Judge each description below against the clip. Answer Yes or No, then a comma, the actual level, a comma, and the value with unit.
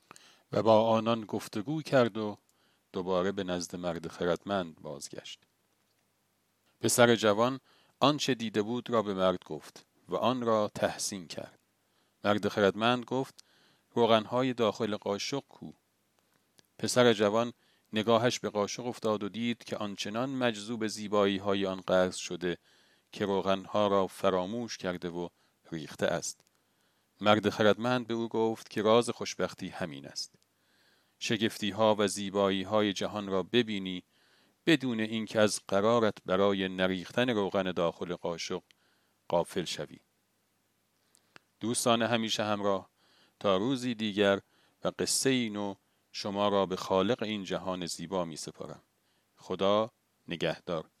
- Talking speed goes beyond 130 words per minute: No, average, 125 wpm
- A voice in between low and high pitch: No, low, 105 Hz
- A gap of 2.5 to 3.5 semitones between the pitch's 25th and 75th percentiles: Yes, average, 3.1 semitones